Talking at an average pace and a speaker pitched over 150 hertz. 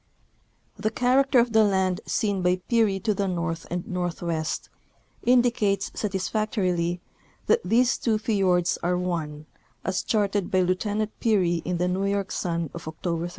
Yes: average, 150 wpm; high, 190 Hz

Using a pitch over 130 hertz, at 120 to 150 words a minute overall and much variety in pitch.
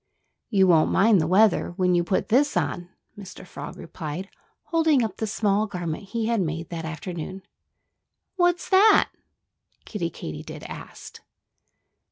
No: high, 190 Hz; average, 140 wpm; average, 4.6 semitones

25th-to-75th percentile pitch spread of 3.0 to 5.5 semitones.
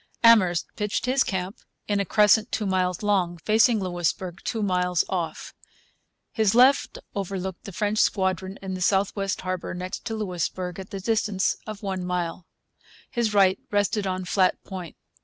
No: narrow, 2.4 semitones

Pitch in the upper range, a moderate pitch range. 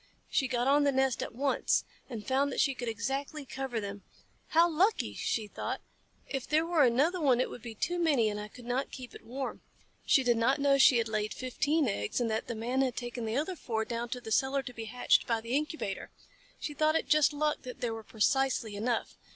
Yes: very high, 255 Hz; average, 3.7 semitones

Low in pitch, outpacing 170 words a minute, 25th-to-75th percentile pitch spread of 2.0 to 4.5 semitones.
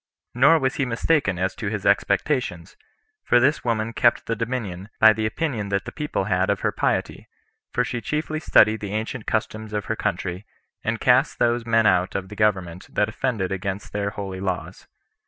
Yes: low, 110 Hz; average, 190 wpm; average, 3.9 semitones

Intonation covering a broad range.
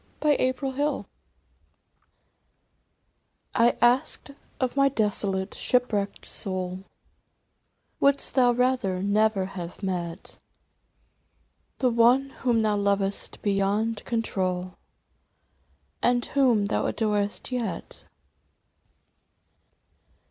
No: average, 4.3 semitones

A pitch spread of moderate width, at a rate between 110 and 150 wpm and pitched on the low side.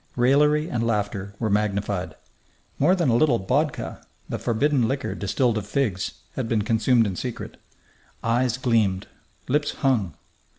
Yes: average, 4.7 semitones; average, 140 wpm; low, 115 Hz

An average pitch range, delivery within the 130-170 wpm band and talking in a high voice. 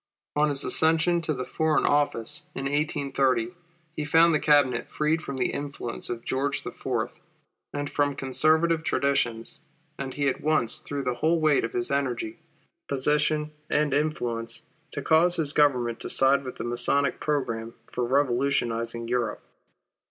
No: average, 3.6 semitones; average, 150 wpm; medium, 140 Hz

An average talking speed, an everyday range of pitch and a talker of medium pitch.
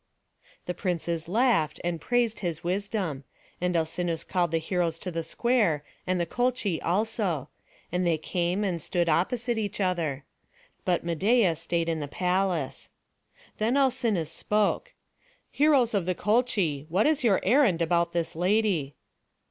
Yes: average, 145 wpm; average, 4.6 semitones; medium, 180 Hz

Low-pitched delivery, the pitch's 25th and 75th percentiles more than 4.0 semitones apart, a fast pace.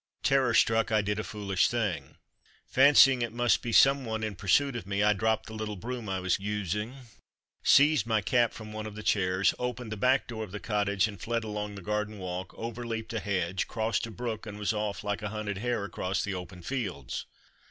No: low, 105 Hz; narrow, 2.6 semitones; fast, 215 wpm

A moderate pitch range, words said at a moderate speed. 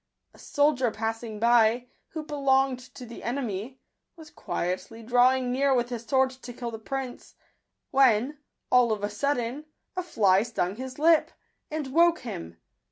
Yes: average, 3.3 semitones; average, 155 wpm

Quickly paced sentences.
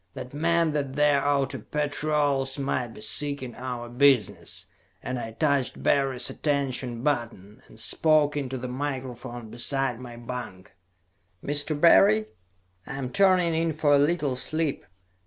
No: average, 140 wpm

